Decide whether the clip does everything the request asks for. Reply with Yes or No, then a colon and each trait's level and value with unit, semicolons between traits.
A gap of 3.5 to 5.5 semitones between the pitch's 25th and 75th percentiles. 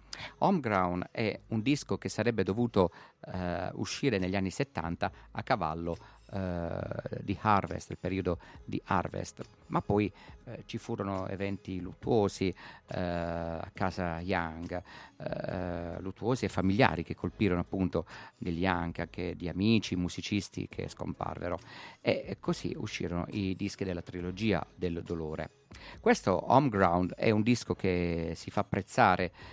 No: narrow, 2.6 semitones